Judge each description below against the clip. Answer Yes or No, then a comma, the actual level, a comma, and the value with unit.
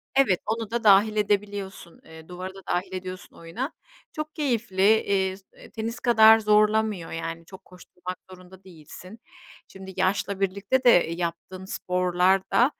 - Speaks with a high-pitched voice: Yes, high, 195 Hz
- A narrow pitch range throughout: No, average, 3.2 semitones